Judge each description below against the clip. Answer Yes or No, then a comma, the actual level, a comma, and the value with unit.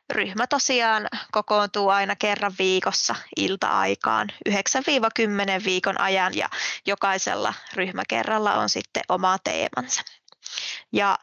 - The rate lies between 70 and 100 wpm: Yes, slow, 95 wpm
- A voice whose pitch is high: Yes, high, 200 Hz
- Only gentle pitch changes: Yes, narrow, 2.1 semitones